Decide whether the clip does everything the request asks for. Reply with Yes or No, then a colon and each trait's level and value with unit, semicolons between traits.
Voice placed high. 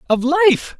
Yes: high, 230 Hz